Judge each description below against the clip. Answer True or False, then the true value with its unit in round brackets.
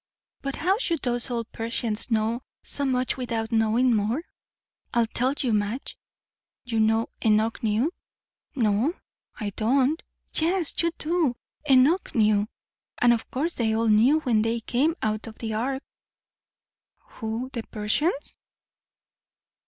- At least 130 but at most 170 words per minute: True (135 wpm)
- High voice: True (235 Hz)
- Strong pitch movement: False (3.6 semitones)